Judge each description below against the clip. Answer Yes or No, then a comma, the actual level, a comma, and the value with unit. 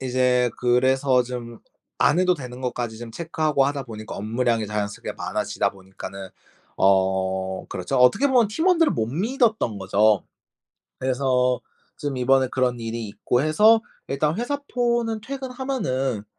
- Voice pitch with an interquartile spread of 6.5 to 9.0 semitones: Yes, wide, 6.8 semitones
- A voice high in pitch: No, low, 125 Hz